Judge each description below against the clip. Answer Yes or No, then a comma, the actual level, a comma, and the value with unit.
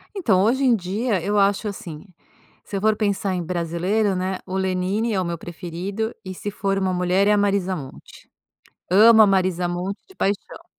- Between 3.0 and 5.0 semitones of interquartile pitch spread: No, narrow, 2.4 semitones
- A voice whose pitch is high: Yes, high, 195 Hz